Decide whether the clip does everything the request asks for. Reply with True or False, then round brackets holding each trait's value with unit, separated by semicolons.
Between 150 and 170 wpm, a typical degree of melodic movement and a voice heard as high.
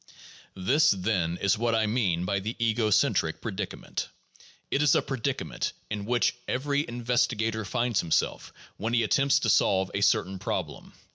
False (155 wpm; 3.8 semitones; 110 Hz)